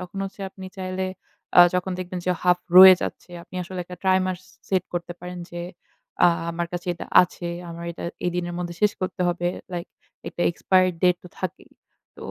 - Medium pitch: Yes, medium, 180 Hz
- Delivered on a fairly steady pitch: Yes, narrow, 1.1 semitones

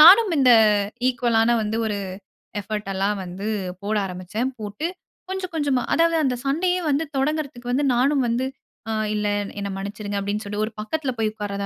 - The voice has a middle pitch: No, high, 230 Hz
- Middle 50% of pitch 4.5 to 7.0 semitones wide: Yes, wide, 5.6 semitones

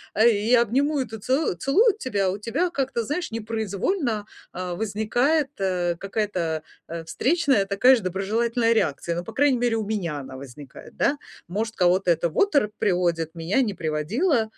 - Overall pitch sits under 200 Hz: No, high, 215 Hz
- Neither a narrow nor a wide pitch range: No, wide, 6.2 semitones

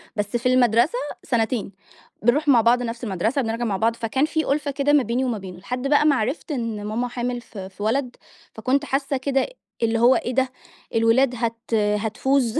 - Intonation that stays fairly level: No, average, 3.1 semitones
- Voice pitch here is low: No, high, 240 Hz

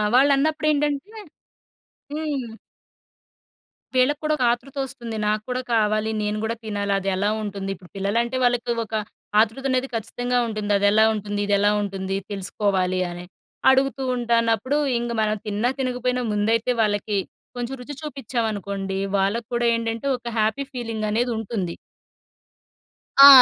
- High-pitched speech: Yes, high, 225 Hz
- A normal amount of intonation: Yes, average, 3.6 semitones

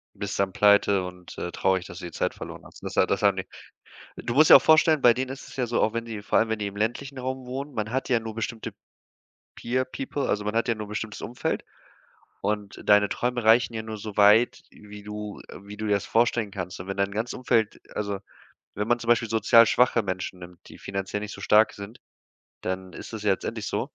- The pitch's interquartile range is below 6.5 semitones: Yes, average, 2.8 semitones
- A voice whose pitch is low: Yes, low, 110 Hz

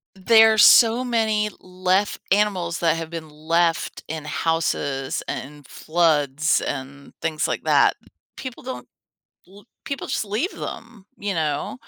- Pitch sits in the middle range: Yes, medium, 175 Hz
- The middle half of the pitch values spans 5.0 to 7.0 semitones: Yes, wide, 5.4 semitones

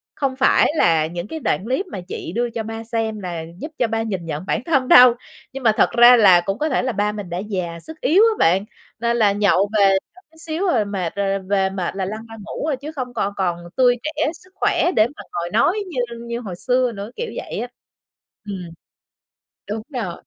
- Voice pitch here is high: Yes, high, 220 Hz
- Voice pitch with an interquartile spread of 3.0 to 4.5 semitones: No, average, 5.0 semitones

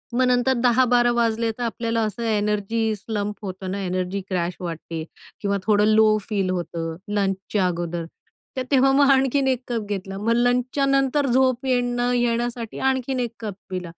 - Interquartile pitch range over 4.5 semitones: No, average, 4.1 semitones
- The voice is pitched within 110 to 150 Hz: No, high, 225 Hz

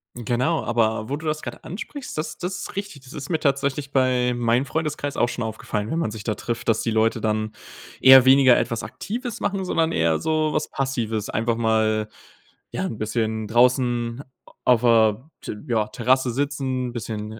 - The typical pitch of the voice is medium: No, low, 125 Hz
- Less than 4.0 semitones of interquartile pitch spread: No, average, 4.3 semitones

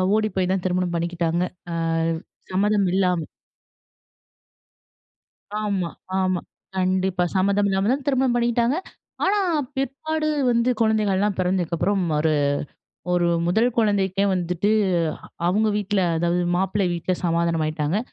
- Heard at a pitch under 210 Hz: Yes, high, 190 Hz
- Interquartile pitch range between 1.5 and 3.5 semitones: Yes, average, 3.2 semitones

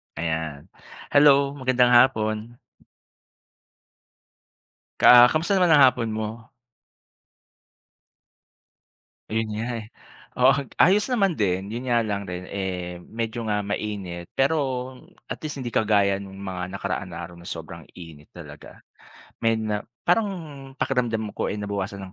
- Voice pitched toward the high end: No, low, 110 Hz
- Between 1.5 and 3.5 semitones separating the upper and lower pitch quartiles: No, average, 4.8 semitones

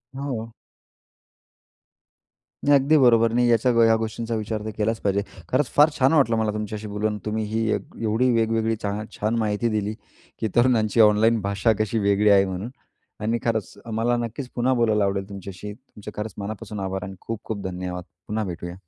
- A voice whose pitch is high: No, low, 110 Hz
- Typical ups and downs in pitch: No, narrow, 2.1 semitones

